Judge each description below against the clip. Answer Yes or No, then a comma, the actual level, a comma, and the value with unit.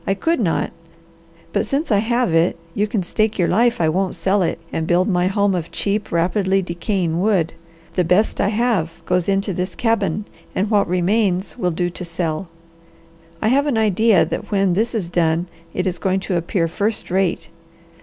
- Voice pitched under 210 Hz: Yes, high, 190 Hz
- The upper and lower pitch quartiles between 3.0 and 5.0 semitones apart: Yes, average, 3.4 semitones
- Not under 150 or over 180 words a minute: No, average, 190 wpm